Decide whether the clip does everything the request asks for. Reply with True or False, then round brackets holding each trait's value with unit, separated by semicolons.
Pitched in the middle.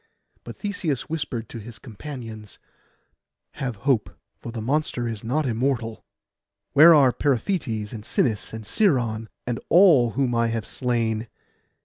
False (120 Hz)